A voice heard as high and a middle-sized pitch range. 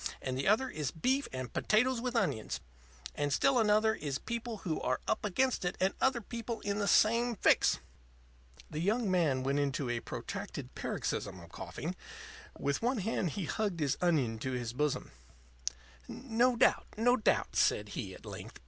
No: high, 200 Hz; wide, 8.5 semitones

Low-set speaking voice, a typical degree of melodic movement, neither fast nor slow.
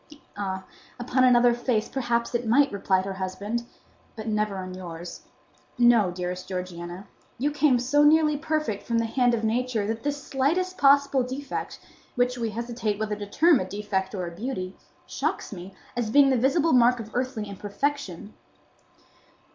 No: high, 235 Hz; average, 4.8 semitones; average, 165 wpm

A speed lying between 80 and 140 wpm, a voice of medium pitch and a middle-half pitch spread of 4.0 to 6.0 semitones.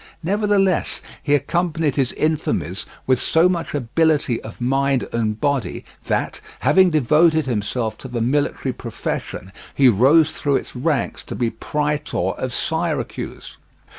Yes: slow, 135 wpm; medium, 145 Hz; average, 4.7 semitones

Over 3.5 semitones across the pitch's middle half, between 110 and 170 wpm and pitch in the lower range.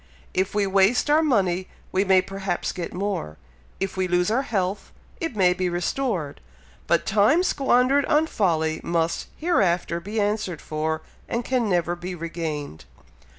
No: average, 4.2 semitones; average, 150 wpm; high, 190 Hz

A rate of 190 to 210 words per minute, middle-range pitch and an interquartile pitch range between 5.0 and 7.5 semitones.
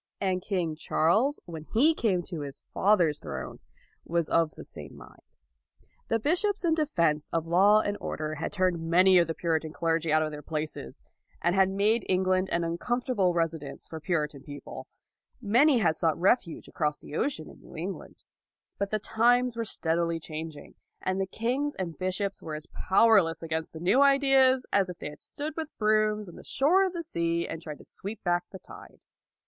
Yes: average, 195 wpm; medium, 180 Hz; wide, 5.4 semitones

